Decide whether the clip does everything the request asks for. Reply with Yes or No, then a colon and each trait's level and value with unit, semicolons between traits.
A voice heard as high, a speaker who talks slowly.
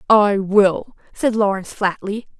Yes: high, 205 Hz; slow, 125 wpm